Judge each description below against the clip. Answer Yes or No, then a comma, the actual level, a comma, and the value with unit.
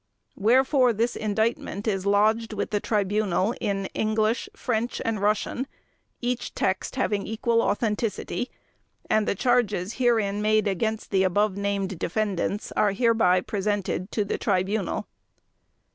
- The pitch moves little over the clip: Yes, narrow, 2.2 semitones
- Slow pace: Yes, slow, 130 wpm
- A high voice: Yes, high, 210 Hz